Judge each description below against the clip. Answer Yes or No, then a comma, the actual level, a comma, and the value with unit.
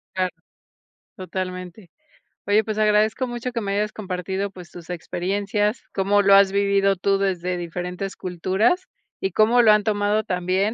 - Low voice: No, high, 195 Hz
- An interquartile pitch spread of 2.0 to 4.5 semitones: Yes, narrow, 2.5 semitones